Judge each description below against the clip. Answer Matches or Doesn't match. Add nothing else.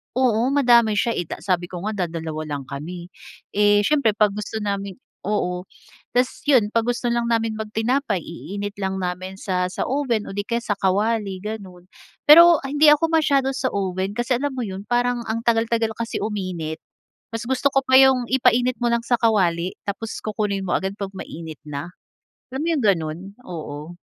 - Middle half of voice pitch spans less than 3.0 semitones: Doesn't match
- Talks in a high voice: Matches